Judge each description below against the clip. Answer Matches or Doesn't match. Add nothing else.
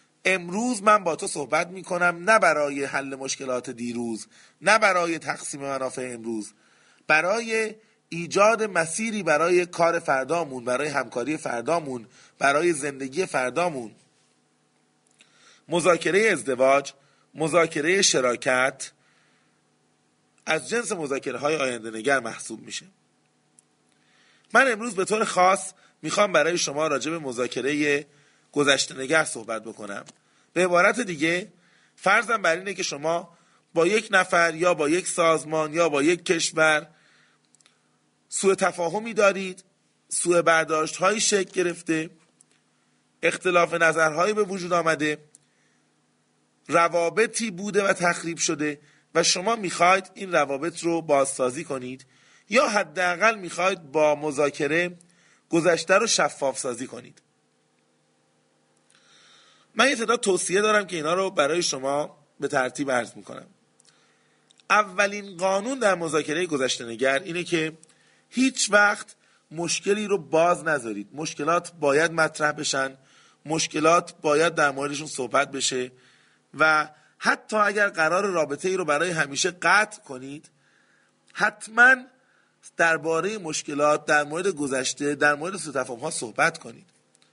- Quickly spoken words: Doesn't match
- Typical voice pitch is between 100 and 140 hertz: Doesn't match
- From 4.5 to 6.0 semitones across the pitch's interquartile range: Matches